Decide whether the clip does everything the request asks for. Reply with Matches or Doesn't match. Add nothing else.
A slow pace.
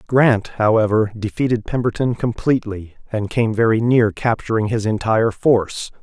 Matches